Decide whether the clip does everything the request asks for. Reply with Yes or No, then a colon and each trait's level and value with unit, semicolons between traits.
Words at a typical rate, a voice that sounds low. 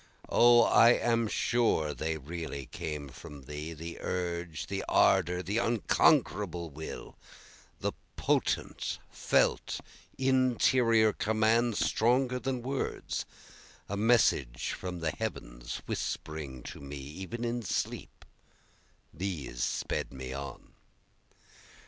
No: slow, 105 wpm; very low, 90 Hz